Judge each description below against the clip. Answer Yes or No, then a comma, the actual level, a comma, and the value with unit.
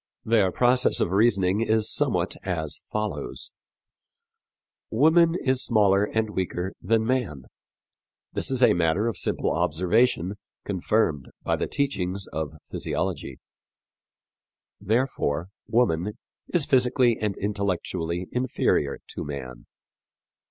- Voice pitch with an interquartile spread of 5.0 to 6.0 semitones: Yes, average, 5.3 semitones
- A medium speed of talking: No, slow, 110 wpm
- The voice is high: No, low, 105 Hz